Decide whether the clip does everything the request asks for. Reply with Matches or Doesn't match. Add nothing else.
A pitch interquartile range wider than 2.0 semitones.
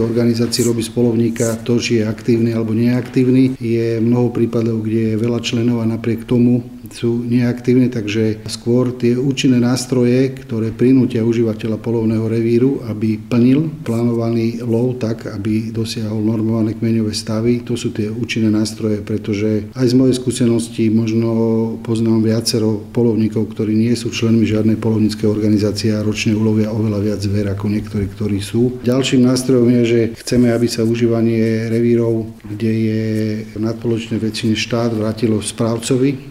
Doesn't match